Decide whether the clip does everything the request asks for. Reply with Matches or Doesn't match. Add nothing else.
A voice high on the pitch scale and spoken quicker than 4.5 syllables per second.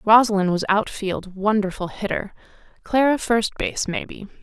Matches